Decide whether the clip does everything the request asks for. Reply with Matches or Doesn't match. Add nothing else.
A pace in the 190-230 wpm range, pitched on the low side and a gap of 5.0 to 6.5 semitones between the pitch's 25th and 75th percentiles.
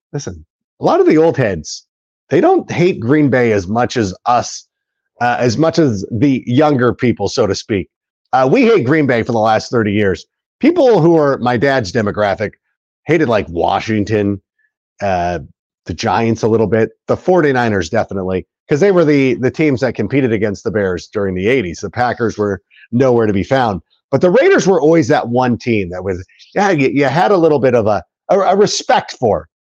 Matches